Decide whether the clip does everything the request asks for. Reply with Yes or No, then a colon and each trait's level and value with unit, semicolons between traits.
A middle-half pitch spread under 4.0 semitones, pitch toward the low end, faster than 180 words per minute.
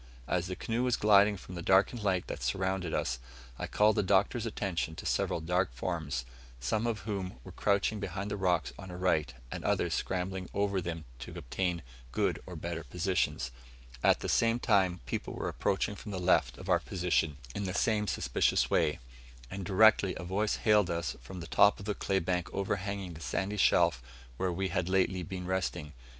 Yes: narrow, 2.6 semitones; very low, 95 Hz; average, 190 wpm